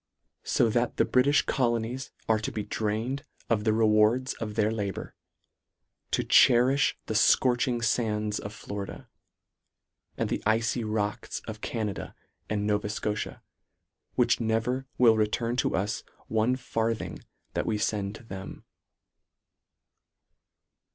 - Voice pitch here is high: No, low, 110 Hz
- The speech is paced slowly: Yes, slow, 125 wpm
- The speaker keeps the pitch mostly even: Yes, narrow, 2.3 semitones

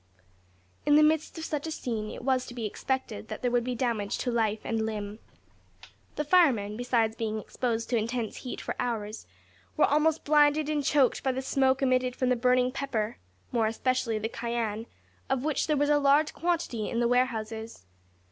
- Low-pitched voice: No, very high, 250 Hz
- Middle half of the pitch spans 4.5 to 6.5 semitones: No, average, 3.8 semitones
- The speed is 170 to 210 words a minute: Yes, average, 190 wpm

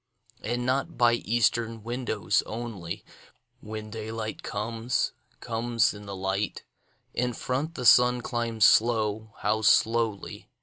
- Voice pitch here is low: Yes, low, 115 Hz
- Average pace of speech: No, slow, 105 wpm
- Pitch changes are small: Yes, narrow, 1.9 semitones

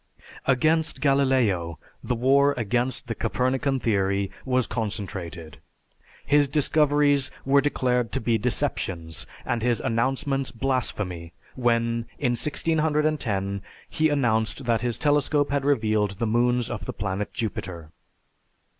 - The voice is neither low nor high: No, low, 120 Hz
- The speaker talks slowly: Yes, slow, 120 wpm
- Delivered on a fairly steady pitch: No, average, 4.6 semitones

